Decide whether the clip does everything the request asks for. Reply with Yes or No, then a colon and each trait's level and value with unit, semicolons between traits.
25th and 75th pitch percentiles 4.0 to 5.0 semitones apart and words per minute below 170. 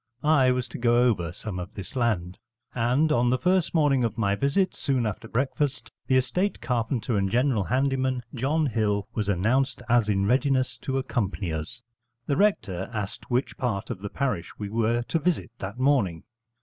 No: average, 4.6 semitones; average, 180 wpm